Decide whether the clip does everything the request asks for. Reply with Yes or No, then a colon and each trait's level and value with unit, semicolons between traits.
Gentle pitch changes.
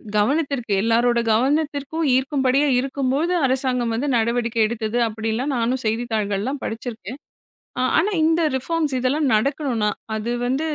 No: average, 3.7 semitones